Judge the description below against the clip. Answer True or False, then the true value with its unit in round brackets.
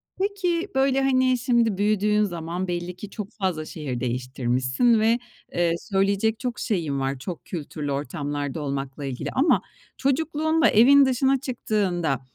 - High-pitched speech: True (195 Hz)